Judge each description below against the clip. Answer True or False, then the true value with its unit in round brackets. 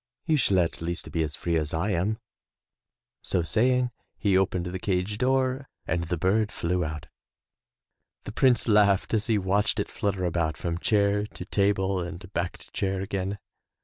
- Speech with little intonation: False (3.3 semitones)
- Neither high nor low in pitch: False (95 Hz)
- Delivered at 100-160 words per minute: False (175 wpm)